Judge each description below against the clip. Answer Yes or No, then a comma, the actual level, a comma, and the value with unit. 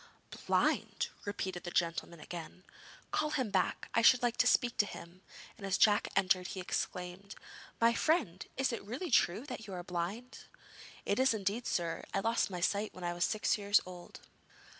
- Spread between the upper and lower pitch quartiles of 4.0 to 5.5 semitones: Yes, average, 4.6 semitones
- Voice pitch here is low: No, high, 200 Hz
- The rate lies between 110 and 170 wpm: No, average, 185 wpm